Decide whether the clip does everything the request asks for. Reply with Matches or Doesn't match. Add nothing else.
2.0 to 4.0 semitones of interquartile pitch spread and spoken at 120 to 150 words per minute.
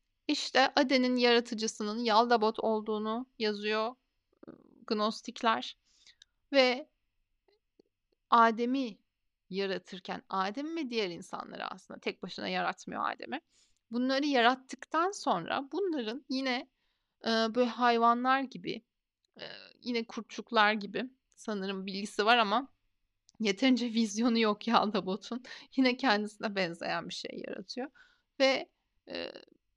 Doesn't match